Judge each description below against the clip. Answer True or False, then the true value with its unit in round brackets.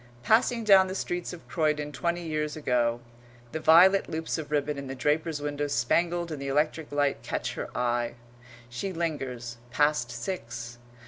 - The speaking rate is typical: True (165 wpm)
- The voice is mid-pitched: True (150 Hz)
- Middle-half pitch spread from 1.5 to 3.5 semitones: False (4.9 semitones)